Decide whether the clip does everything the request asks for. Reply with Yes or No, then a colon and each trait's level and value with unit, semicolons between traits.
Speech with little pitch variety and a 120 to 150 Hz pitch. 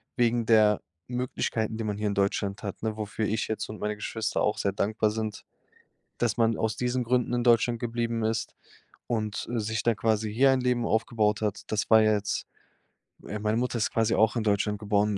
No: narrow, 1.7 semitones; low, 110 Hz